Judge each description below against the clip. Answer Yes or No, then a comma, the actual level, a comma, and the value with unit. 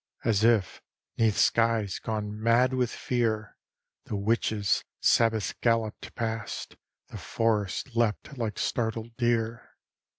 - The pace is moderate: No, slow, 110 wpm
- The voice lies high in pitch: No, low, 115 Hz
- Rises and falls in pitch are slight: Yes, narrow, 1.5 semitones